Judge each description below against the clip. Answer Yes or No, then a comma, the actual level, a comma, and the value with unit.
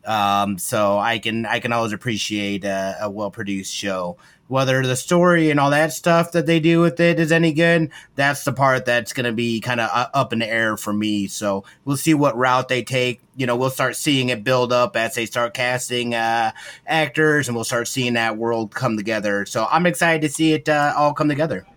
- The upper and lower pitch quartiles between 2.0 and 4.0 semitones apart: No, average, 4.7 semitones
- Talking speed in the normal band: No, fast, 225 wpm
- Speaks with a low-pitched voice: Yes, low, 125 Hz